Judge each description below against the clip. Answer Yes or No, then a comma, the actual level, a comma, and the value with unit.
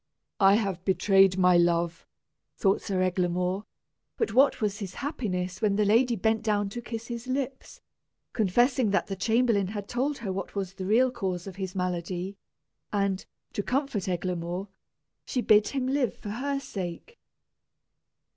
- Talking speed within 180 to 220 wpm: No, average, 155 wpm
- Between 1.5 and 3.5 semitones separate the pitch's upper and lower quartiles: No, average, 4.3 semitones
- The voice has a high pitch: Yes, high, 200 Hz